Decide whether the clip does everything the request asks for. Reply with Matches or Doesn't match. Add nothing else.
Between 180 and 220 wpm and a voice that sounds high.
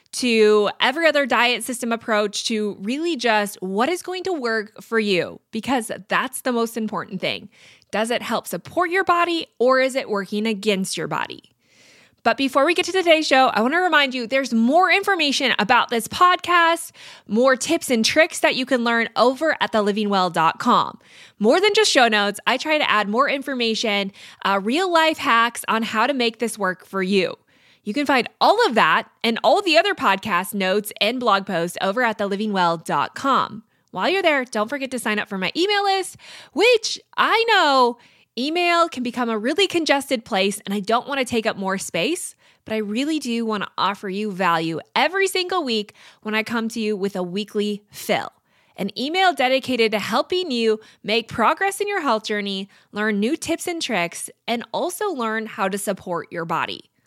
Matches